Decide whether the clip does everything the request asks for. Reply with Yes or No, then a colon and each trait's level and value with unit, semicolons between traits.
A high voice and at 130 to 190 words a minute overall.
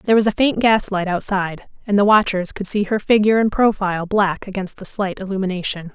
No: high, 200 Hz; average, 200 wpm